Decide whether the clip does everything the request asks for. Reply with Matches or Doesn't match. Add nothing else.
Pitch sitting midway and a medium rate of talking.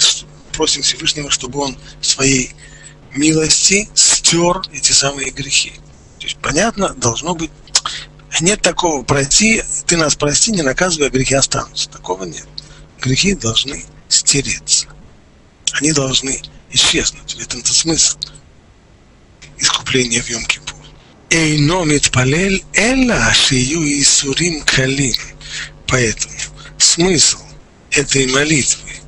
Doesn't match